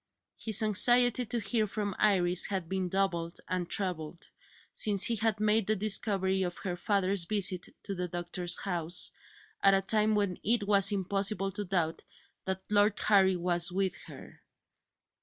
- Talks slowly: No, average, 160 wpm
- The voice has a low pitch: No, high, 195 Hz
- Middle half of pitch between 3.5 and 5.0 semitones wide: No, average, 2.7 semitones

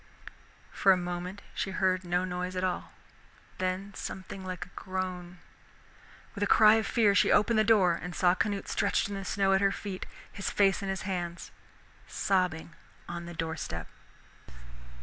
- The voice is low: No, medium, 185 Hz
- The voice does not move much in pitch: Yes, narrow, 1.8 semitones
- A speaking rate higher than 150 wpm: Yes, average, 170 wpm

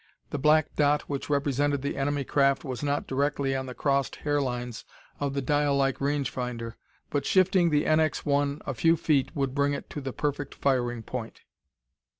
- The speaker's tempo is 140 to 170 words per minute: No, average, 185 wpm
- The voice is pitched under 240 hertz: Yes, medium, 140 Hz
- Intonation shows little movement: Yes, narrow, 1.6 semitones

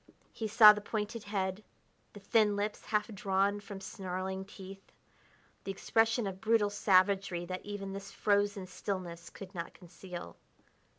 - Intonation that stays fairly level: Yes, narrow, 1.7 semitones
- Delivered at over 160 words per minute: No, average, 140 wpm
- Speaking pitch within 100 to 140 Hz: No, high, 200 Hz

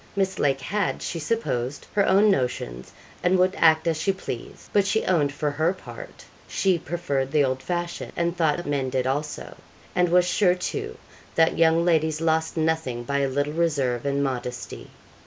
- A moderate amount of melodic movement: Yes, average, 4.3 semitones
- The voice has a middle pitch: Yes, medium, 160 Hz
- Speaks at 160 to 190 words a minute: Yes, average, 180 wpm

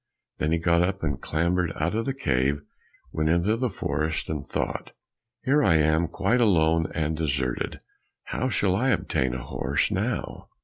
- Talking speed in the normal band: Yes, average, 170 wpm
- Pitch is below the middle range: Yes, very low, 80 Hz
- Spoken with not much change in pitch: No, average, 4.1 semitones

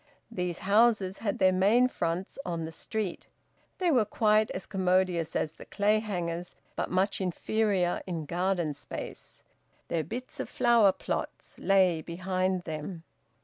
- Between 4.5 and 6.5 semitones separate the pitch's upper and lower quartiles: No, average, 3.4 semitones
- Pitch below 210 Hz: Yes, medium, 185 Hz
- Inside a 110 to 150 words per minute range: Yes, average, 140 wpm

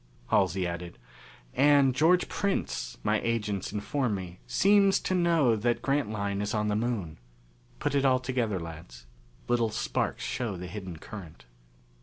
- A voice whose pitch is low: Yes, low, 110 Hz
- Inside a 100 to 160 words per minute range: Yes, average, 145 wpm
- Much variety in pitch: Yes, wide, 6.3 semitones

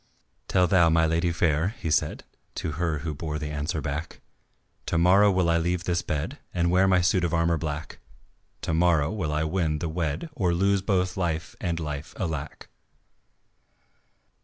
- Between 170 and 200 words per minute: Yes, average, 175 wpm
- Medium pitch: No, very low, 85 Hz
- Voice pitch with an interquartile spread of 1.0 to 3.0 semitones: Yes, narrow, 2.5 semitones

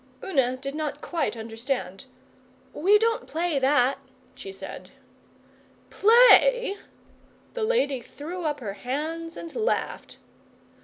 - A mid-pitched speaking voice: No, very high, 305 Hz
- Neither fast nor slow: No, slow, 110 wpm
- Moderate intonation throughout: No, wide, 6.9 semitones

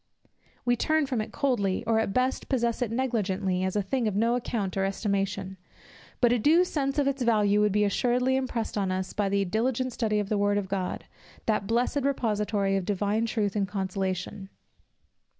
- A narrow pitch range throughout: No, average, 3.9 semitones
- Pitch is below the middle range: No, high, 210 Hz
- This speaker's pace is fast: No, average, 190 wpm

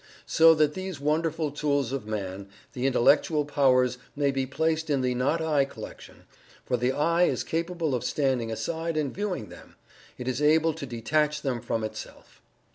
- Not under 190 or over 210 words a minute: No, average, 175 wpm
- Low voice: No, medium, 145 Hz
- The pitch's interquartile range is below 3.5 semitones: No, average, 4.0 semitones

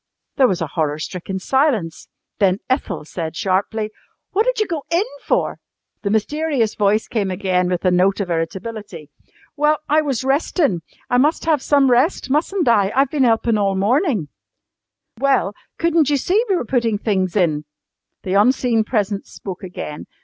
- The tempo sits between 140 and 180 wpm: Yes, average, 165 wpm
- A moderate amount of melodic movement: No, wide, 6.9 semitones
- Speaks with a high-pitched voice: Yes, high, 220 Hz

